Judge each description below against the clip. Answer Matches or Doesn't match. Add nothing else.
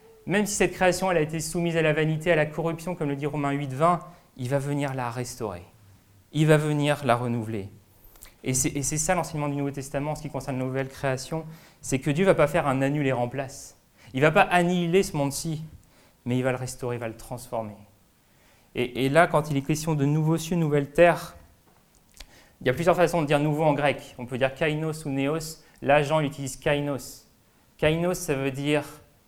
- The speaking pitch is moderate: Matches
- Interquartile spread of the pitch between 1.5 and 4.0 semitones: Matches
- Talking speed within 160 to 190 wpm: Doesn't match